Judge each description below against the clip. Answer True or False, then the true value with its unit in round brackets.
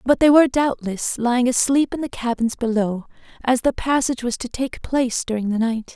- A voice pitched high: True (245 Hz)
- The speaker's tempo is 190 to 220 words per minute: True (200 wpm)